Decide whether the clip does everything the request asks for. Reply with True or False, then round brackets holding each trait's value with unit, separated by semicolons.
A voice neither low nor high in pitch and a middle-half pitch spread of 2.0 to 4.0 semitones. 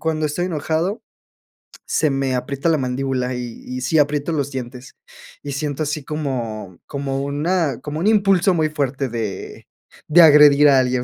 True (145 Hz; 3.3 semitones)